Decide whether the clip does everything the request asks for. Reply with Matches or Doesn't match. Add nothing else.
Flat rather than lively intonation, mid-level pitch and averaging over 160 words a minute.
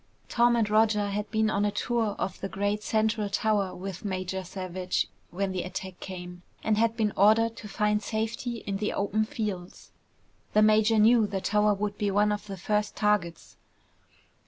Doesn't match